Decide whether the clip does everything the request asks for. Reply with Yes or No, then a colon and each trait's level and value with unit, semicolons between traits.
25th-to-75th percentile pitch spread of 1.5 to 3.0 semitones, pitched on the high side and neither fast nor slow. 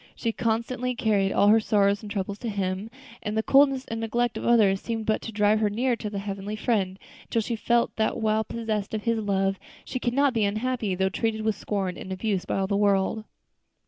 No: narrow, 2.4 semitones; high, 215 Hz; fast, 220 wpm